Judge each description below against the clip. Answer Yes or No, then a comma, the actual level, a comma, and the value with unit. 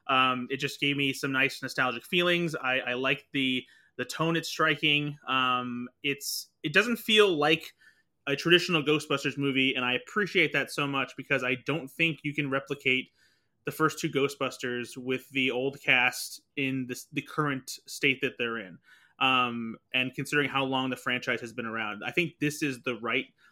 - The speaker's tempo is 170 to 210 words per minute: Yes, average, 185 wpm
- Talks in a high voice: No, low, 135 Hz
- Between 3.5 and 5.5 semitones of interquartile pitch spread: No, narrow, 2.6 semitones